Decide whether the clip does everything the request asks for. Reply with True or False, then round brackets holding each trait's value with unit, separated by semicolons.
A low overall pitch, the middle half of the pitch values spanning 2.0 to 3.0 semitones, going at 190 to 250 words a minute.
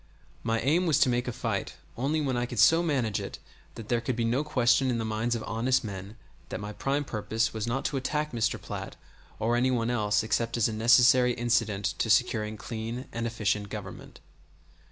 True (120 Hz; 2.5 semitones; 205 wpm)